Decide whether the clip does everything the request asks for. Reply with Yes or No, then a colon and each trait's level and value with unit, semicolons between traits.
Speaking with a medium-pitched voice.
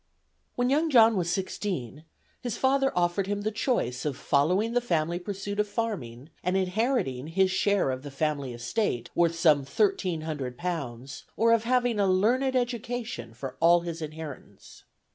Yes: medium, 180 Hz